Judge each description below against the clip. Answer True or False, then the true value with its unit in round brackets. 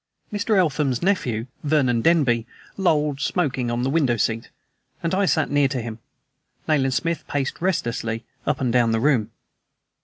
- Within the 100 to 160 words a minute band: True (155 wpm)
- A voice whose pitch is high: False (135 Hz)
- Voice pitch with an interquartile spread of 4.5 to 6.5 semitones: True (5.3 semitones)